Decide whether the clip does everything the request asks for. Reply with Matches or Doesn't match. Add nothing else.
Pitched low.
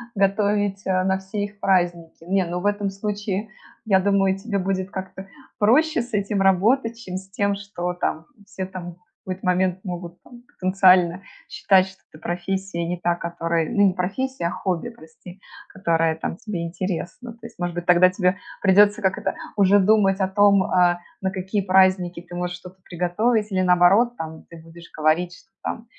Doesn't match